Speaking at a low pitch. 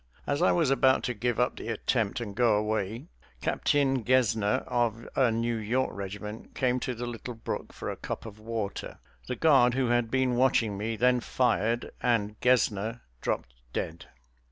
Yes: low, 120 Hz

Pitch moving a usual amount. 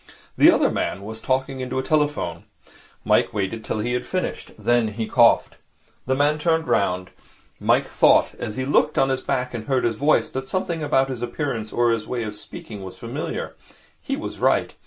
Yes: average, 4.0 semitones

